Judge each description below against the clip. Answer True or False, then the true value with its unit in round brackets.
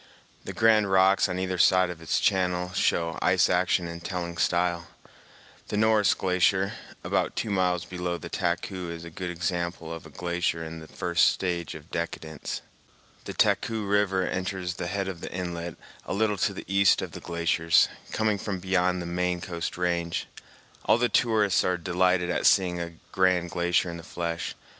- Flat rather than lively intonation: True (1.8 semitones)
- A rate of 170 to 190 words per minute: True (180 wpm)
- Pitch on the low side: True (90 Hz)